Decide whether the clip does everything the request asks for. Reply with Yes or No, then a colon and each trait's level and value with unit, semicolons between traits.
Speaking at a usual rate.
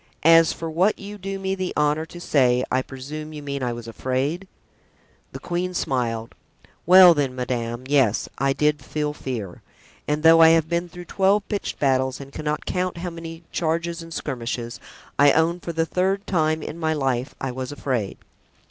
Yes: average, 185 wpm